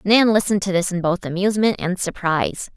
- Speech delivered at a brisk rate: No, average, 195 wpm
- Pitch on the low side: No, high, 190 Hz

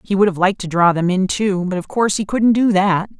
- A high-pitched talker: Yes, high, 195 Hz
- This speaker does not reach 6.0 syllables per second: No, 6.1 syllables/s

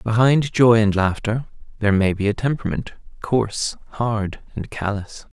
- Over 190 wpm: No, average, 145 wpm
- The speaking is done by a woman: No, male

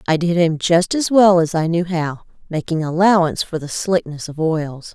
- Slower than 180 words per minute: No, fast, 205 wpm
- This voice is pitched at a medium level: Yes, medium, 170 Hz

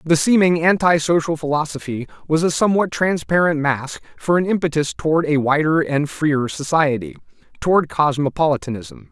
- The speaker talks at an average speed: No, slow, 125 wpm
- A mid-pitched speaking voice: Yes, medium, 155 Hz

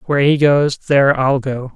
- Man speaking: Yes, male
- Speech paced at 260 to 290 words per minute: No, fast, 205 wpm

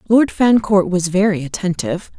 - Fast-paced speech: No, slow, 135 wpm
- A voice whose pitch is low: No, high, 190 Hz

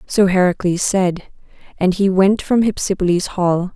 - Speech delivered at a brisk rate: No, average, 145 wpm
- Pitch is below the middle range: No, medium, 185 Hz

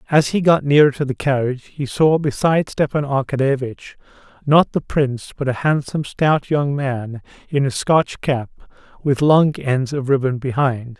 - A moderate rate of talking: Yes, average, 170 wpm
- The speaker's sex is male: Yes, male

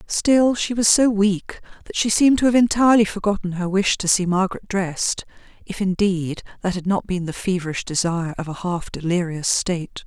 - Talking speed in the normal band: Yes, average, 185 wpm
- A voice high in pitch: Yes, high, 195 Hz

